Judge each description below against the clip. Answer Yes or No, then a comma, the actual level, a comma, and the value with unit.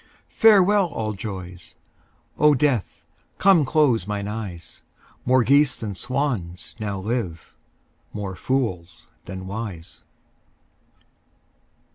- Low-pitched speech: Yes, low, 110 Hz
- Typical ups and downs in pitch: No, wide, 6.5 semitones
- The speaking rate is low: Yes, slow, 95 wpm